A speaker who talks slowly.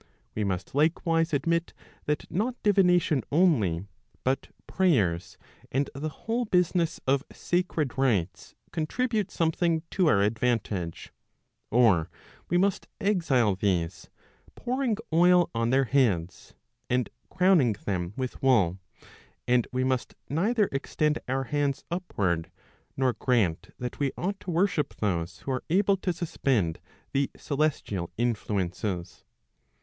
Yes: slow, 125 wpm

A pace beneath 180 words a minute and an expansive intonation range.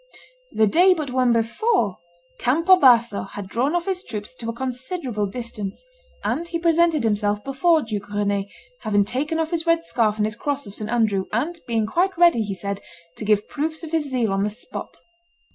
No: average, 195 wpm; wide, 7.5 semitones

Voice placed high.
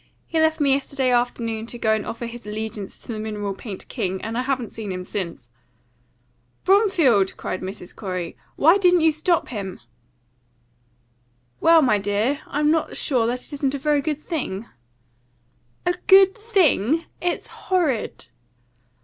Yes: very high, 250 Hz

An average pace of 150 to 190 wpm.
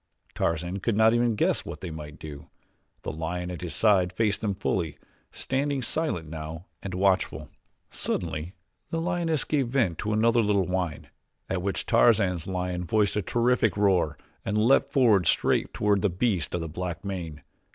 Yes: average, 170 wpm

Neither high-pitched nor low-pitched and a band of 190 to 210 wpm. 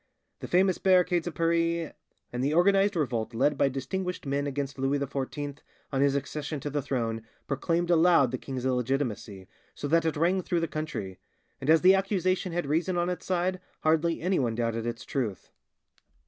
No: medium, 150 Hz; average, 175 wpm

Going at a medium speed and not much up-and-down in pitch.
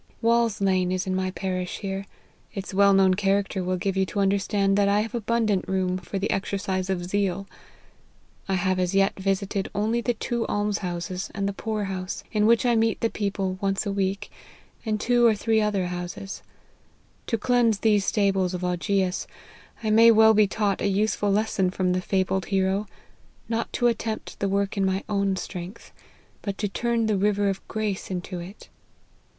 Yes: average, 185 wpm; narrow, 2.1 semitones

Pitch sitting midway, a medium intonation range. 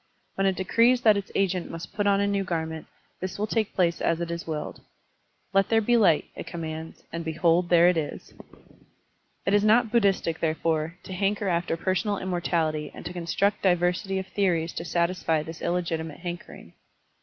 Yes: medium, 175 Hz; average, 3.1 semitones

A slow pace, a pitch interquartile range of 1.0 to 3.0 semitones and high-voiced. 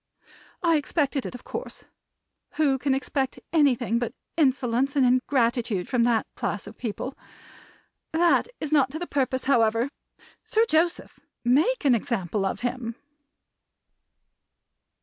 No: slow, 130 wpm; average, 3.7 semitones; very high, 260 Hz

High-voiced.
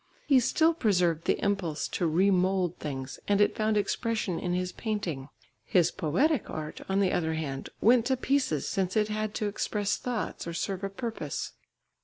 Yes: high, 195 Hz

